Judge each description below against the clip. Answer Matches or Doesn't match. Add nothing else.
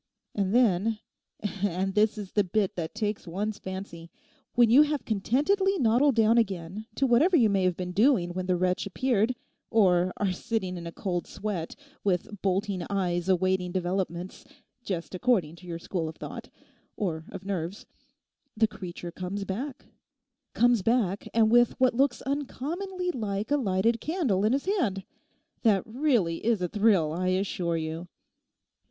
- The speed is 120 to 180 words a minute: Matches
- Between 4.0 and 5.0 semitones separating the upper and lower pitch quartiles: Matches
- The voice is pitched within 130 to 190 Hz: Doesn't match